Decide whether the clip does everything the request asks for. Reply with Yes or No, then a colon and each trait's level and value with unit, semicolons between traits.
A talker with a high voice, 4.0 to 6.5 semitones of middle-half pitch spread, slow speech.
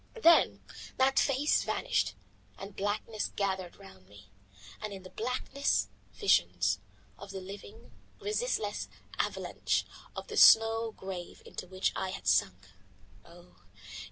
Yes: high, 195 Hz; average, 4.3 semitones; slow, 125 wpm